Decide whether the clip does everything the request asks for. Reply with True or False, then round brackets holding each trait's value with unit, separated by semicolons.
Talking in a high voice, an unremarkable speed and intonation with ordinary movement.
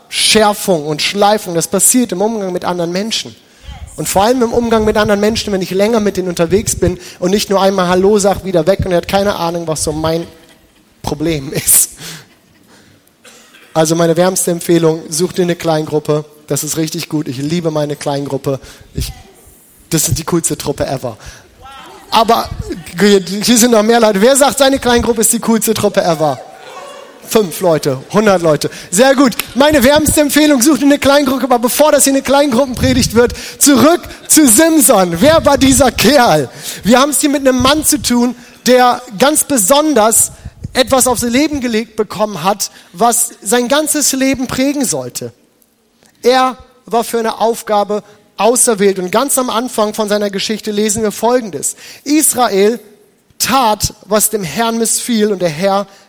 False (215 Hz; 170 wpm; 6.1 semitones)